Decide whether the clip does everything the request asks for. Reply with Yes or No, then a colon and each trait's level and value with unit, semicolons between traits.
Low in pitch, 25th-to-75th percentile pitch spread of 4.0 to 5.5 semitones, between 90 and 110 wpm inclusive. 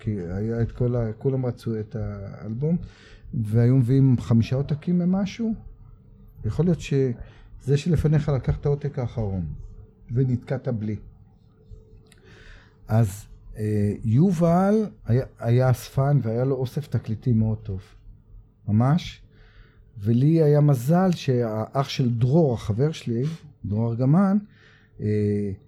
Yes: low, 115 Hz; average, 4.5 semitones; average, 105 wpm